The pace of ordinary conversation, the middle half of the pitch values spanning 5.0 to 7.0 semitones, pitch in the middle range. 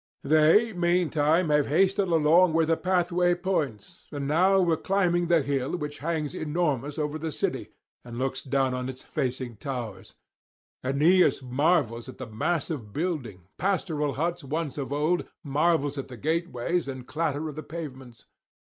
No: average, 160 wpm; average, 4.4 semitones; medium, 150 Hz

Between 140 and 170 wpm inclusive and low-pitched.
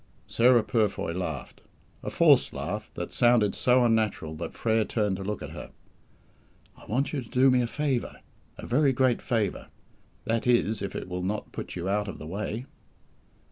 No: average, 180 wpm; low, 110 Hz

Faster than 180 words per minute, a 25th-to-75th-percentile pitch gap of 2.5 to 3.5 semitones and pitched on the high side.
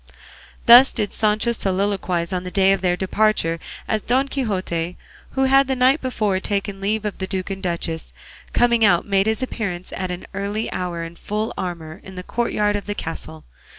Yes: average, 190 wpm; average, 3.2 semitones; high, 200 Hz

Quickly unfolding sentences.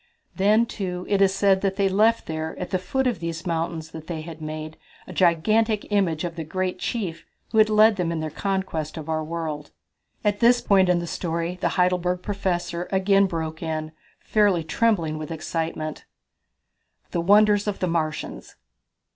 No: average, 170 wpm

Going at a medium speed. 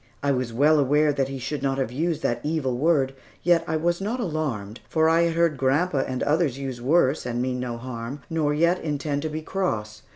No: fast, 215 wpm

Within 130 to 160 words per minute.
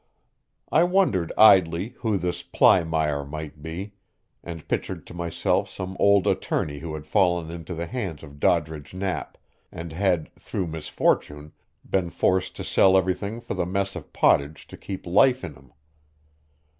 Yes: average, 155 wpm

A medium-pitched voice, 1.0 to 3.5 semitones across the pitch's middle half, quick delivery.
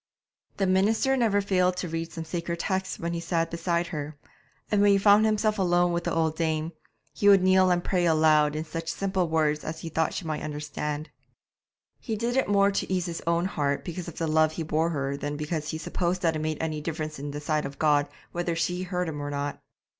Yes: medium, 165 Hz; average, 3.1 semitones; fast, 230 wpm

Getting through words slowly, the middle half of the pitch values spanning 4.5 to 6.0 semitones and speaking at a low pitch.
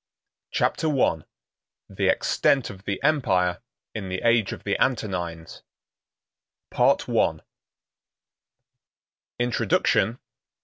Yes: slow, 85 wpm; average, 4.8 semitones; low, 105 Hz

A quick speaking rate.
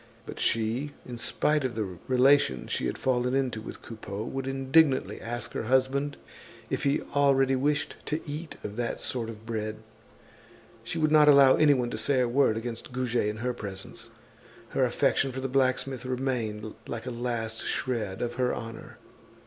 No: average, 175 wpm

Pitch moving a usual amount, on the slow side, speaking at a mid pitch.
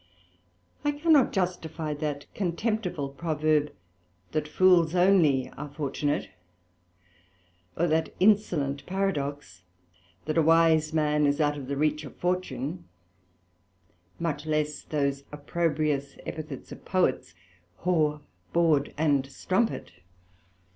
Yes: average, 3.1 semitones; slow, 105 wpm; medium, 155 Hz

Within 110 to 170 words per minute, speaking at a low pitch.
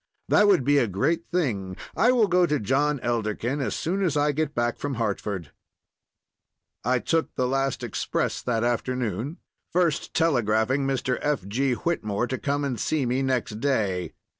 Yes: average, 165 wpm; low, 130 Hz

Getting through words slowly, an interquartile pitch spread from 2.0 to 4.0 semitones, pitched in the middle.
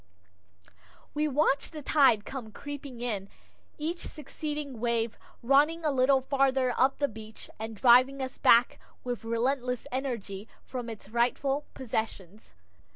No: slow, 130 wpm; average, 3.5 semitones; very high, 255 Hz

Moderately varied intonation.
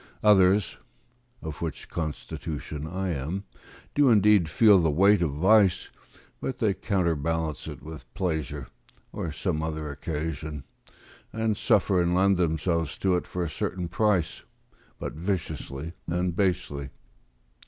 Yes: average, 3.8 semitones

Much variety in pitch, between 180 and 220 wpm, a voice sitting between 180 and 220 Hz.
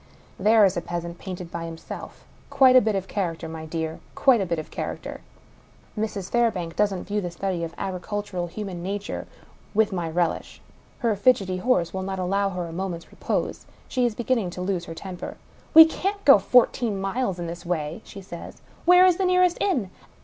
No: average, 4.3 semitones; average, 200 wpm; high, 190 Hz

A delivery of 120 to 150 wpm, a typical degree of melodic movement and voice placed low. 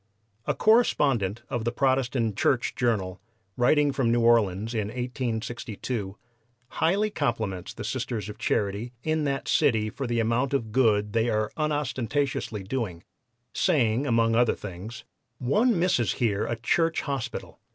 Yes: average, 140 wpm; average, 4.0 semitones; low, 120 Hz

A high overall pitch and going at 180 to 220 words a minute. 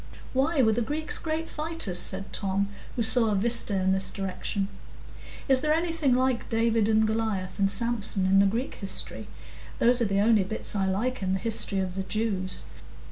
Yes: high, 220 Hz; average, 190 wpm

